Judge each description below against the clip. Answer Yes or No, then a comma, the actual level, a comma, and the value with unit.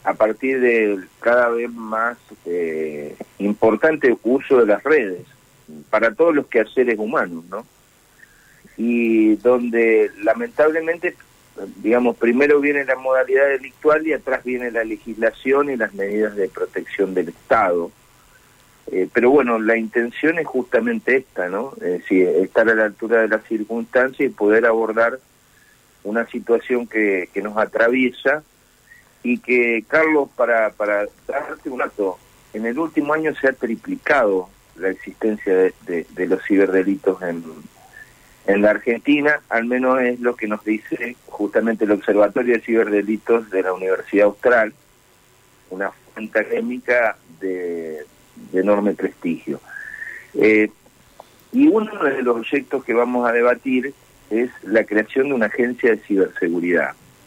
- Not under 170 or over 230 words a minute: No, average, 140 wpm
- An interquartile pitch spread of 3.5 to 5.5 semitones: Yes, average, 3.8 semitones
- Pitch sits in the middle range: No, low, 115 Hz